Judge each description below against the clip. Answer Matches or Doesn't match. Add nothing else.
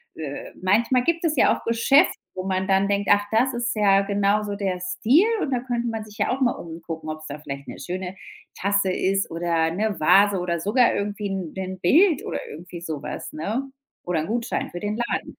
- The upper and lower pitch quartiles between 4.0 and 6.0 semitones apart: Matches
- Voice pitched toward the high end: Matches